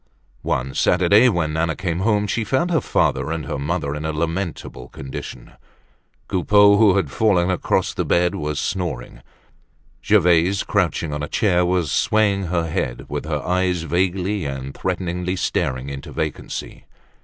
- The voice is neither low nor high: No, very low, 85 Hz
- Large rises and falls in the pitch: No, average, 4.1 semitones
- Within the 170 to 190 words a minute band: No, average, 155 wpm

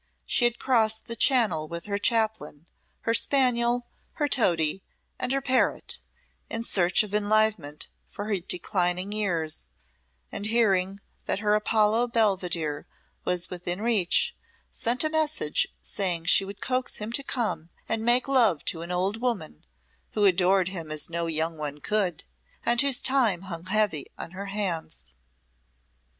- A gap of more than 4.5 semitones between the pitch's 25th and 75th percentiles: Yes, average, 5.1 semitones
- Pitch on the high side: Yes, high, 205 Hz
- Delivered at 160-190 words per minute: No, average, 150 wpm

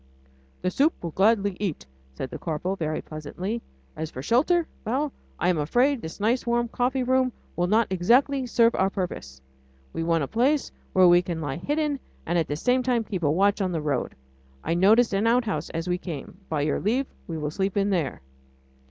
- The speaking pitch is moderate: No, high, 195 Hz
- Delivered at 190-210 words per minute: Yes, fast, 205 wpm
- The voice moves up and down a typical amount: No, wide, 6.7 semitones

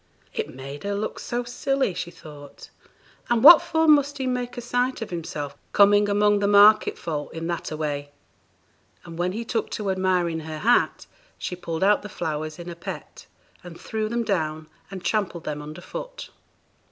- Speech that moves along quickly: No, average, 185 wpm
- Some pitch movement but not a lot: No, wide, 5.8 semitones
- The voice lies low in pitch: No, high, 190 Hz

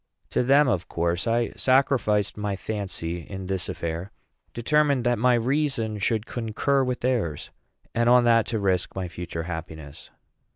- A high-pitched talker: No, low, 110 Hz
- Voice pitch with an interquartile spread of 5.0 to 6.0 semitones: Yes, wide, 5.4 semitones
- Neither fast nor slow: Yes, average, 155 wpm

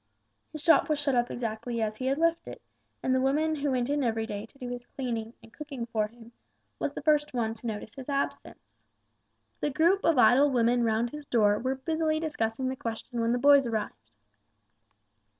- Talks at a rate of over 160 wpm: Yes, fast, 205 wpm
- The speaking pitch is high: Yes, very high, 250 Hz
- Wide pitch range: No, average, 4.1 semitones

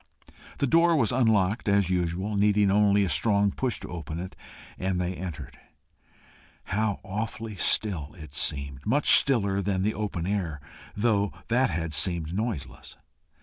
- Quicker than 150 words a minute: No, average, 145 wpm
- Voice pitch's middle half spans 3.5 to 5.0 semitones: Yes, average, 3.8 semitones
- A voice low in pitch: Yes, low, 100 Hz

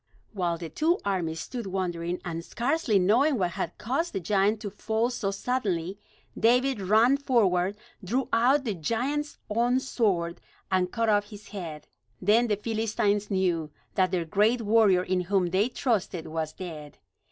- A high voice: Yes, high, 205 Hz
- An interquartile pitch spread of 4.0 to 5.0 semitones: Yes, average, 4.6 semitones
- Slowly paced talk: No, average, 160 wpm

